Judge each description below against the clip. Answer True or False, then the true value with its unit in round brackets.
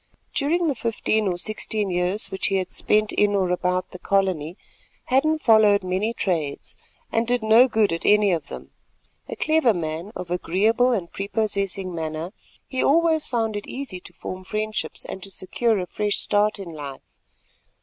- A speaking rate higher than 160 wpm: True (170 wpm)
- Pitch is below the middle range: False (205 Hz)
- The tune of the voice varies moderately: True (3.6 semitones)